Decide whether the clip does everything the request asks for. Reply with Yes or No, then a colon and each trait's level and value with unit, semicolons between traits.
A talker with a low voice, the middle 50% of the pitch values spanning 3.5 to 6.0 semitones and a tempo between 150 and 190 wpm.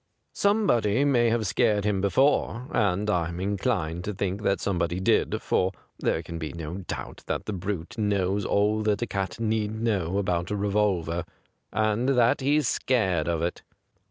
Yes: low, 100 Hz; average, 3.8 semitones; average, 165 wpm